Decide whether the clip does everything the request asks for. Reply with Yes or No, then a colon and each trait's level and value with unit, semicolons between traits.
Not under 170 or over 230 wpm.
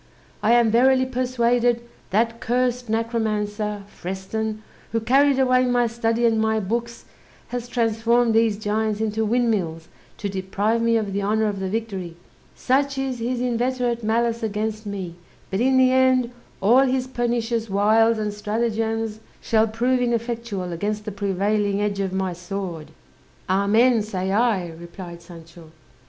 No: average, 145 wpm